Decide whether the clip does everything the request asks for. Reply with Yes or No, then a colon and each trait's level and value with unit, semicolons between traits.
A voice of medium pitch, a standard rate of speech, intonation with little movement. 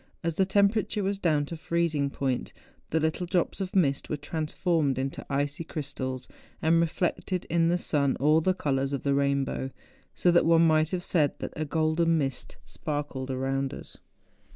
No: medium, 155 Hz; average, 175 wpm; average, 3.4 semitones